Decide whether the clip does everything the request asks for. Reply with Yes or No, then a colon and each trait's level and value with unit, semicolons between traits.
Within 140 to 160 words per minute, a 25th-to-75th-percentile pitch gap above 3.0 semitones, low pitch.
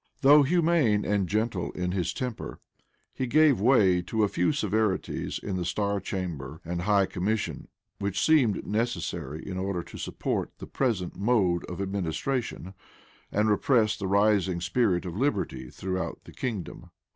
Yes: average, 150 wpm; average, 4.1 semitones; low, 100 Hz